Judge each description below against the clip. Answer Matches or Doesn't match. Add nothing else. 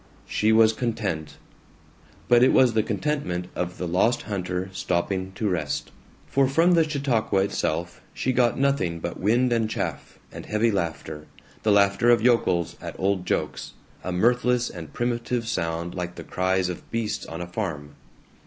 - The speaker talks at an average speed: Matches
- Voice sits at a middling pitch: Doesn't match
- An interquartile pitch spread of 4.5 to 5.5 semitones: Matches